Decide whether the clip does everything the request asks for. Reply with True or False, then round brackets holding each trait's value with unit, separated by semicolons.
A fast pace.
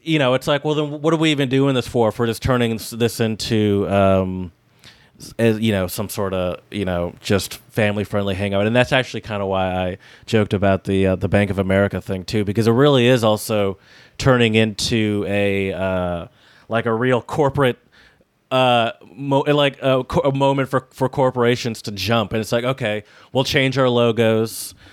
False (195 wpm)